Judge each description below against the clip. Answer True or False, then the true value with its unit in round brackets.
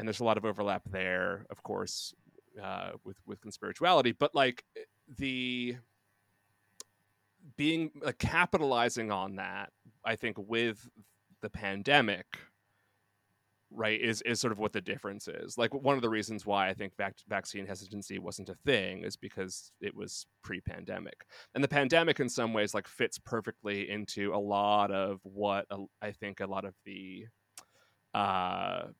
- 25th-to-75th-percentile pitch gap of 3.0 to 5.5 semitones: False (2.4 semitones)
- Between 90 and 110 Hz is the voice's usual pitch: True (100 Hz)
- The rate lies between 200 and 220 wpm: False (155 wpm)